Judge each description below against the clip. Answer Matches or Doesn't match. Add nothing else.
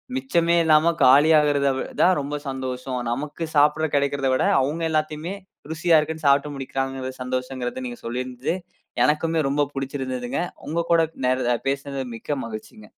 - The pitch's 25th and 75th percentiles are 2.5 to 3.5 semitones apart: Matches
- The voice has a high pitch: Doesn't match